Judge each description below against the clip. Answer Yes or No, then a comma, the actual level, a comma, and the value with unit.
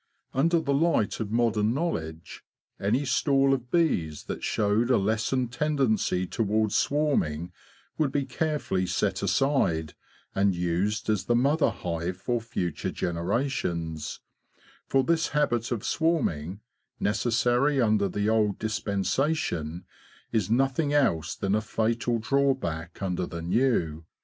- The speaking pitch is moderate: No, low, 110 Hz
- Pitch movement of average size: No, wide, 6.8 semitones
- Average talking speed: No, slow, 125 wpm